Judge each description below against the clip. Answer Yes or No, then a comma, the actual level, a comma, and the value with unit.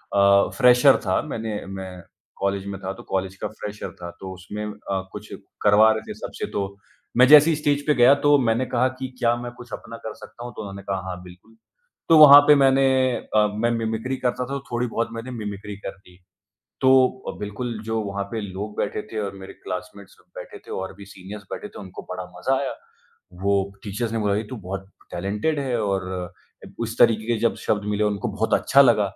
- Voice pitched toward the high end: No, low, 105 Hz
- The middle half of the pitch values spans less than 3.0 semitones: No, average, 3.7 semitones